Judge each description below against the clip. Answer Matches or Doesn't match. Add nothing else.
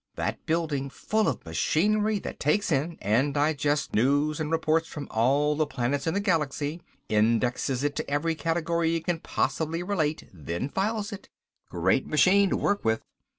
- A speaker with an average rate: Matches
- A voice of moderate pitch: Matches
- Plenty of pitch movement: Doesn't match